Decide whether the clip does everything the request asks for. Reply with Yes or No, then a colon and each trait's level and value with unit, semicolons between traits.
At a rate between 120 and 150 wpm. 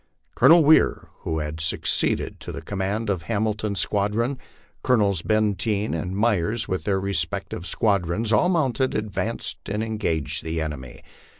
Yes: slow, 135 wpm